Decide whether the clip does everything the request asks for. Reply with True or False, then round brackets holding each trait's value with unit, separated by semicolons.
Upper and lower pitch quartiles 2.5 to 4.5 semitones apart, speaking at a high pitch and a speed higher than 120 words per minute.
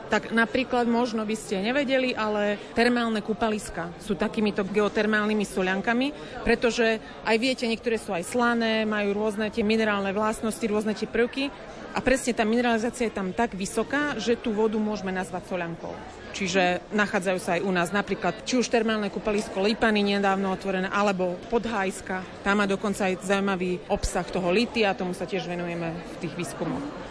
True (2.9 semitones; 215 Hz; 165 wpm)